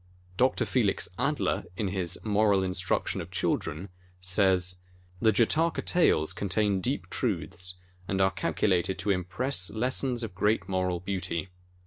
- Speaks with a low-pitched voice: Yes, very low, 95 Hz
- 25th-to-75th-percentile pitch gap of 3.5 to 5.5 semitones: No, average, 3.0 semitones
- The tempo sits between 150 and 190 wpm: No, average, 140 wpm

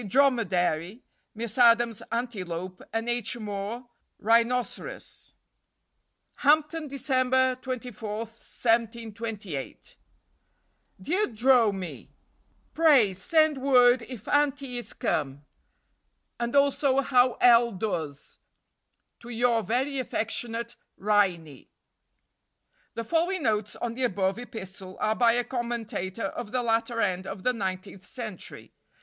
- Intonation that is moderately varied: Yes, average, 3.7 semitones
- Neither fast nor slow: No, slow, 110 wpm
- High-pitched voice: Yes, high, 230 Hz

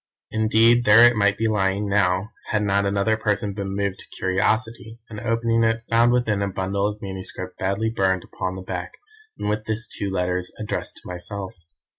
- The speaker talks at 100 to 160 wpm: No, average, 185 wpm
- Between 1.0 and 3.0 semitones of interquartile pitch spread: Yes, narrow, 2.6 semitones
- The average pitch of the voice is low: Yes, low, 100 Hz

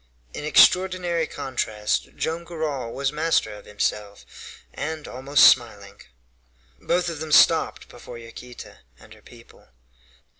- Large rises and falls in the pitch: Yes, wide, 5.9 semitones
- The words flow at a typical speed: No, slow, 120 wpm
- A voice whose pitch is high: No, medium, 140 Hz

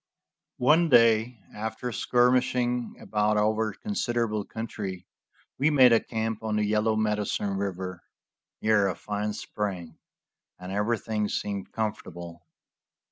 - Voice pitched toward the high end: No, low, 110 Hz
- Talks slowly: Yes, slow, 115 wpm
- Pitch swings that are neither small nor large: No, narrow, 2.2 semitones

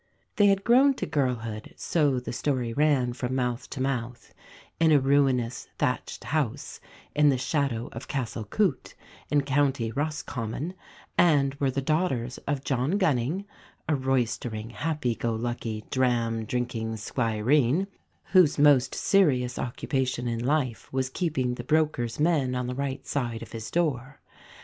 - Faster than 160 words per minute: No, average, 145 wpm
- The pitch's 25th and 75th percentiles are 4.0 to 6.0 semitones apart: No, average, 3.5 semitones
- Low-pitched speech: Yes, low, 130 Hz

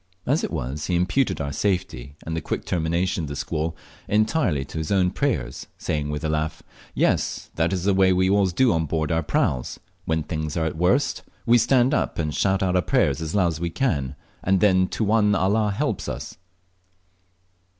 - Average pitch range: Yes, average, 4.3 semitones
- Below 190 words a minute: No, average, 200 wpm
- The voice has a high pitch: No, very low, 90 Hz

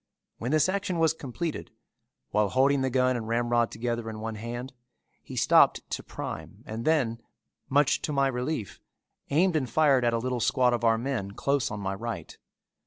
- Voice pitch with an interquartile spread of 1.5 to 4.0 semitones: Yes, average, 3.5 semitones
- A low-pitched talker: Yes, low, 125 Hz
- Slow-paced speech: No, average, 180 wpm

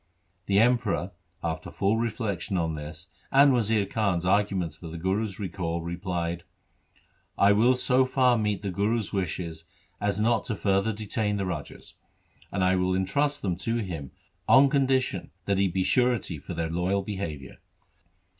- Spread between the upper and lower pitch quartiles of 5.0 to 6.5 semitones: No, average, 4.2 semitones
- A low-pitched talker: Yes, low, 100 Hz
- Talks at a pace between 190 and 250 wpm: No, average, 160 wpm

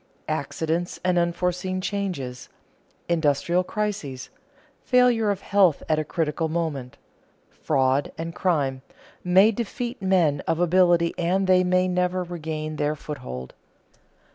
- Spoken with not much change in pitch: No, average, 3.5 semitones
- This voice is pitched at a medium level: Yes, medium, 175 Hz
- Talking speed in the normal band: No, slow, 115 wpm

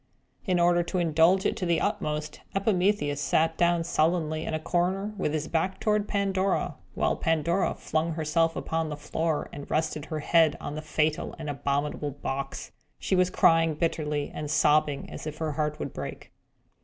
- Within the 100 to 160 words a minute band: No, average, 175 wpm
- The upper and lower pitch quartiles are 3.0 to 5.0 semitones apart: No, narrow, 2.4 semitones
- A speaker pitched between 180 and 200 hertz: No, medium, 160 Hz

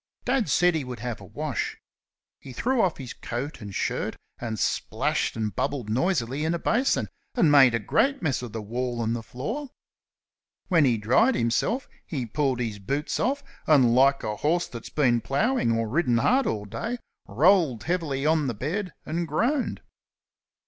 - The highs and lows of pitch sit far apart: Yes, wide, 7.0 semitones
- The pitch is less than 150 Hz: Yes, medium, 140 Hz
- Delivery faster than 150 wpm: Yes, average, 180 wpm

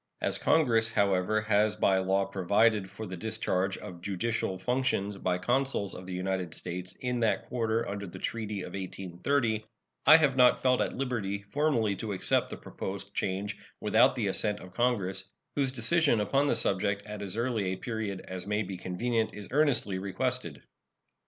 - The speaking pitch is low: Yes, low, 105 Hz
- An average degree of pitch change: Yes, average, 3.9 semitones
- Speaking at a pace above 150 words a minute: Yes, average, 170 wpm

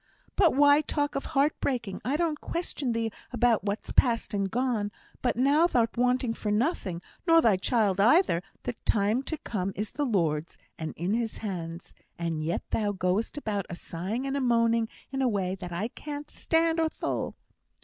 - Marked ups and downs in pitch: Yes, wide, 5.8 semitones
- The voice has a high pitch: Yes, high, 230 Hz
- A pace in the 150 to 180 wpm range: No, average, 190 wpm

